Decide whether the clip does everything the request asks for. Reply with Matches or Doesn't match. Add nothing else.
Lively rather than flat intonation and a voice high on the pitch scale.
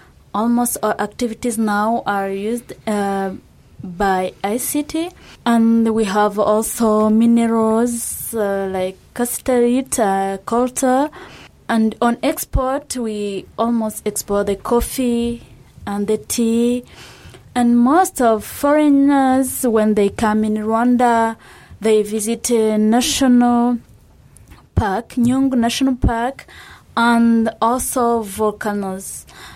Doesn't match